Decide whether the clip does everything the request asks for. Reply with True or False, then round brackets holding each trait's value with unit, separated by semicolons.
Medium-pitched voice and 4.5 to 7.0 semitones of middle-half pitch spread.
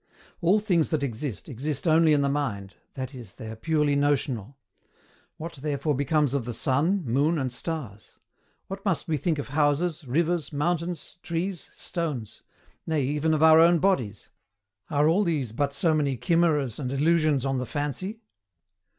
False (150 Hz; 3.7 semitones)